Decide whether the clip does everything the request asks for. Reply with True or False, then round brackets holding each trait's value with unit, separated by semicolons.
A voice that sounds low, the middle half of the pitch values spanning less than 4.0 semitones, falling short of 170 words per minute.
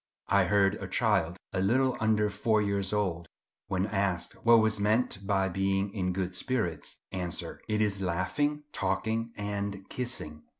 True (100 Hz; 2.5 semitones; 155 wpm)